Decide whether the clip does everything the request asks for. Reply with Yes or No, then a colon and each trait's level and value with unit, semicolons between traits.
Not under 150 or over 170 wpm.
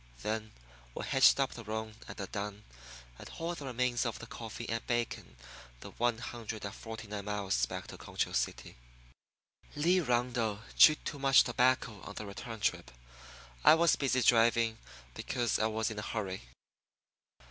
Yes: average, 165 wpm